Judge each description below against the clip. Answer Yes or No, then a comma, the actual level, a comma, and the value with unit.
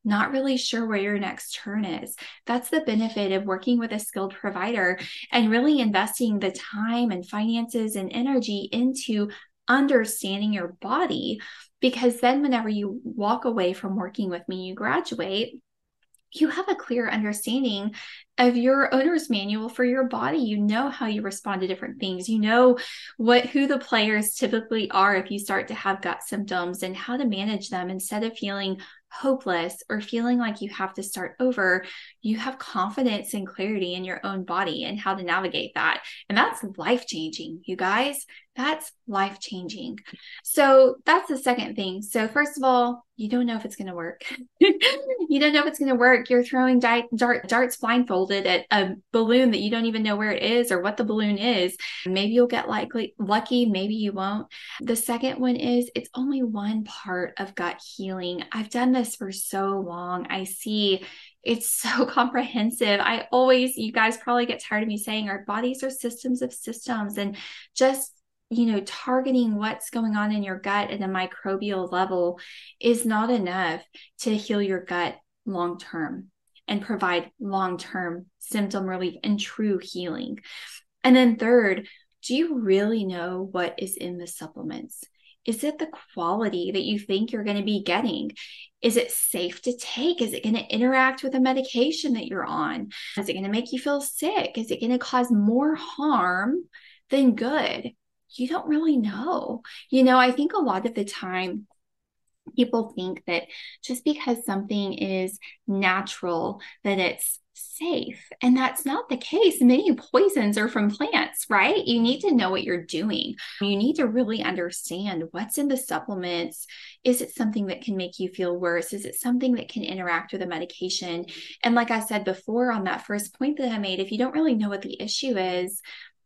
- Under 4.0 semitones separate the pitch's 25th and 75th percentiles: No, average, 4.6 semitones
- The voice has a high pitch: Yes, high, 225 Hz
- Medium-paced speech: Yes, average, 185 wpm